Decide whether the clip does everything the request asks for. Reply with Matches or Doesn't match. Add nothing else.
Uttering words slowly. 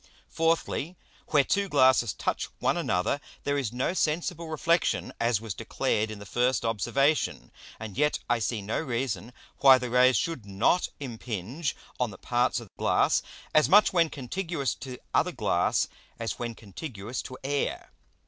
Doesn't match